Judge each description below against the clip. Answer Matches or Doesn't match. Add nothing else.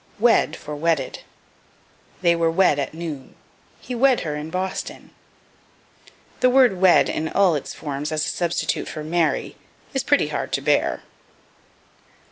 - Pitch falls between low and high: Matches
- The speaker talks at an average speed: Matches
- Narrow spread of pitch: Doesn't match